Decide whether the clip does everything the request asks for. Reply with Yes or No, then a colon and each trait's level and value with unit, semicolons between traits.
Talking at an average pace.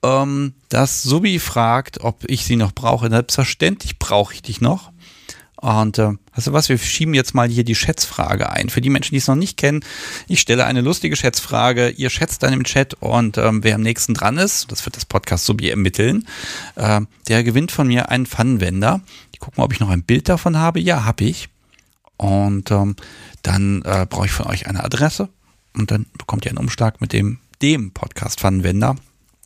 No: fast, 200 wpm